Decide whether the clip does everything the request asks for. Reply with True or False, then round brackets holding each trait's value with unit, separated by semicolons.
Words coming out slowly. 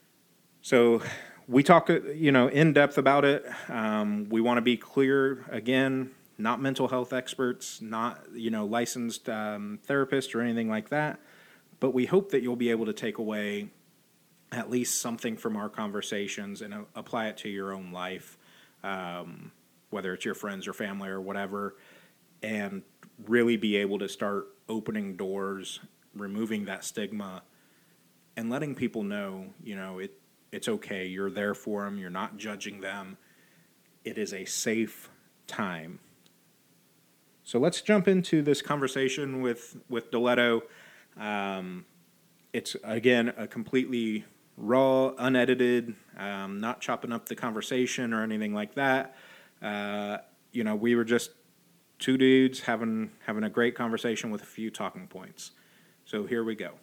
False (150 wpm)